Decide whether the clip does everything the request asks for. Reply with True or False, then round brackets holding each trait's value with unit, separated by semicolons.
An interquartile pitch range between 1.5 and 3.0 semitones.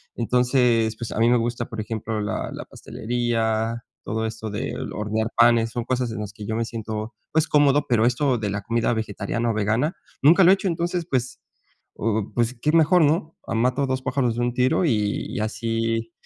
True (2.5 semitones)